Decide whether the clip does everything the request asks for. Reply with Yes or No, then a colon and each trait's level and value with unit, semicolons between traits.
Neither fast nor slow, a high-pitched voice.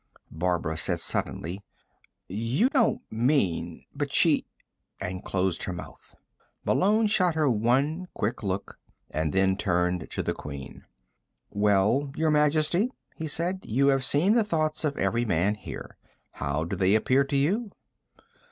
No: average, 145 wpm; low, 120 Hz